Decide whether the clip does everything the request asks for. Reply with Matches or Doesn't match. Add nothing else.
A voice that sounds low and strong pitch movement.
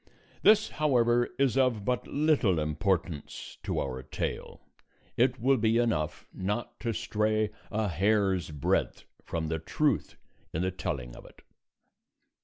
Matches